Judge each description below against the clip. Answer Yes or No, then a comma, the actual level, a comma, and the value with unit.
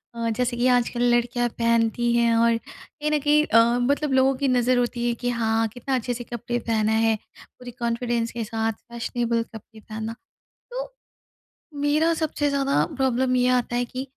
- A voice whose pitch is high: Yes, high, 240 Hz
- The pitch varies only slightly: Yes, narrow, 1.9 semitones